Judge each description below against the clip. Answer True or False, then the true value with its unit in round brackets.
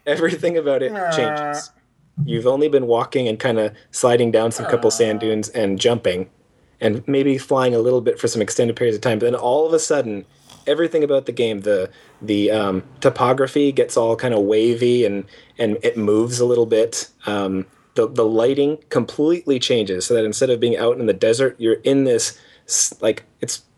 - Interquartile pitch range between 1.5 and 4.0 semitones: False (4.9 semitones)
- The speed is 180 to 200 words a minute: True (195 wpm)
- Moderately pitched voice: False (125 Hz)